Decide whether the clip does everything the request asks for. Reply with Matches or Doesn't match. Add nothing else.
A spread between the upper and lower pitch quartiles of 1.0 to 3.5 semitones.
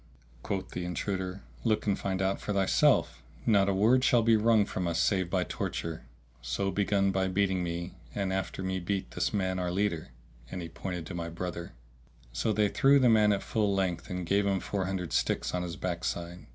Matches